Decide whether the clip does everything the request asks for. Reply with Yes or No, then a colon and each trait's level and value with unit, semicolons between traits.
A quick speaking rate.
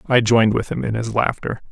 Yes: fast, 245 wpm